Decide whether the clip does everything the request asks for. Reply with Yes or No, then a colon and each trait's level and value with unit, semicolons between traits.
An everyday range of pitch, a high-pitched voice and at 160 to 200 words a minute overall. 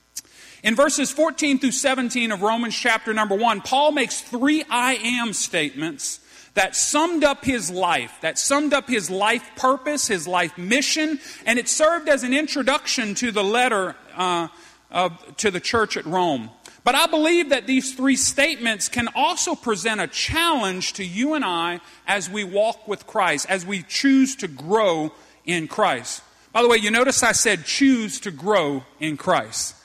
No: wide, 6.3 semitones; high, 235 Hz; average, 175 wpm